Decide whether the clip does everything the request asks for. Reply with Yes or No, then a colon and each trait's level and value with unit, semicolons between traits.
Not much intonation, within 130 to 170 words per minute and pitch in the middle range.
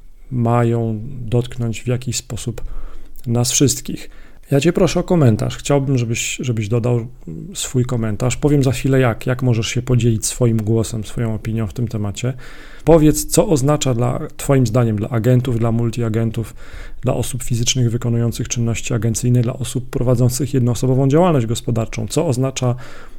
No: narrow, 2.1 semitones; average, 150 wpm; low, 120 Hz